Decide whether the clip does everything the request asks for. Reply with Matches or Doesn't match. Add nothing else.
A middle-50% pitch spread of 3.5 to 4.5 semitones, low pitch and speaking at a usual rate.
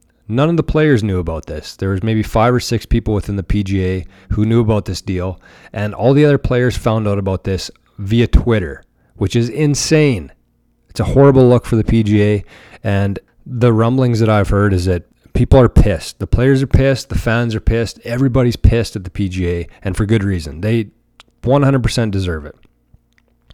Matches